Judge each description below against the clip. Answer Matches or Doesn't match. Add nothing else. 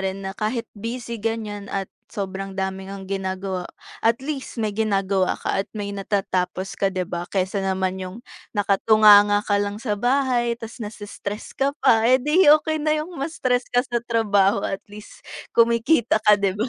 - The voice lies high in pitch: Matches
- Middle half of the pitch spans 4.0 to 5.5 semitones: Doesn't match